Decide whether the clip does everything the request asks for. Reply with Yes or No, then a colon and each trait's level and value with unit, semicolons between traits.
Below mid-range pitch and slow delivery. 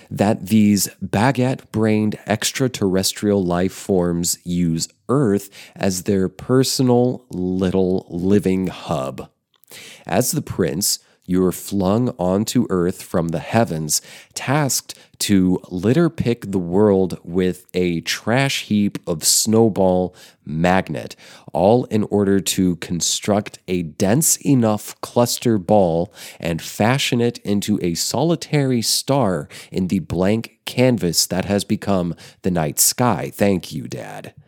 Yes: low, 100 Hz; slow, 120 wpm